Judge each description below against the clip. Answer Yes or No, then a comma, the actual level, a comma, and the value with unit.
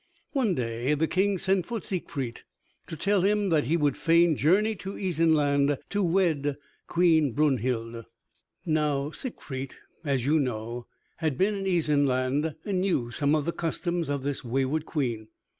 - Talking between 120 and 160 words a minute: Yes, average, 155 wpm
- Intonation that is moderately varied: Yes, average, 4.8 semitones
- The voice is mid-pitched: Yes, medium, 155 Hz